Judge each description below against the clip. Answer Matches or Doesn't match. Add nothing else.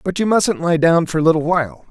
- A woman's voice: Doesn't match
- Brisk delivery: Matches